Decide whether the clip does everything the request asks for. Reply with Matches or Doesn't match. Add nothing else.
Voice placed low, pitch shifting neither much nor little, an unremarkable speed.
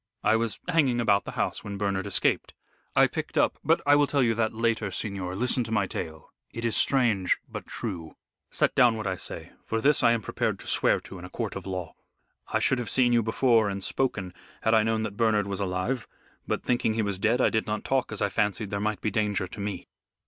Doesn't match